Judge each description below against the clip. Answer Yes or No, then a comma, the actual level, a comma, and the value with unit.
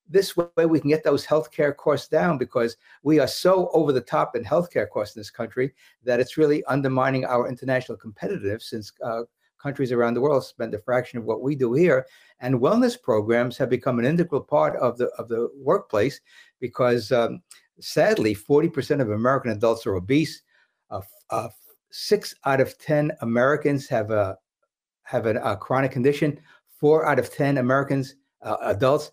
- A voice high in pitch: No, low, 135 Hz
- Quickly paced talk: No, average, 175 wpm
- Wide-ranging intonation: No, average, 4.0 semitones